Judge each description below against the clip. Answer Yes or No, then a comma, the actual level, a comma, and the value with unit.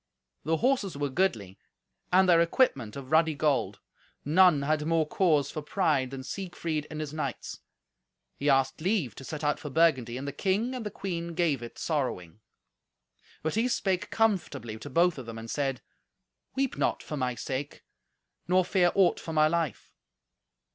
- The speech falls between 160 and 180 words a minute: Yes, average, 170 wpm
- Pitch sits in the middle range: Yes, medium, 155 Hz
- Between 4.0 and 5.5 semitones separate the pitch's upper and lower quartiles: Yes, average, 4.9 semitones